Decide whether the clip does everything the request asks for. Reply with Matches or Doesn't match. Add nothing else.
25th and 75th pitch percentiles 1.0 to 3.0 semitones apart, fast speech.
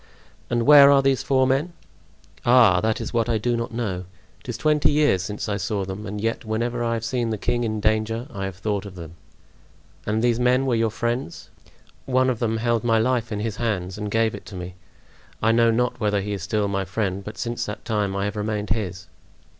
Matches